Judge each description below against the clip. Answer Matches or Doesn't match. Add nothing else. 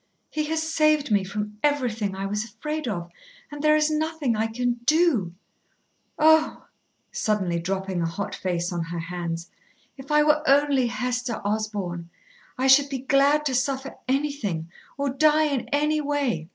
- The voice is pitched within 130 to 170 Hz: Doesn't match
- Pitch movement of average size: Doesn't match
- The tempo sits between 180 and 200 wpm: Doesn't match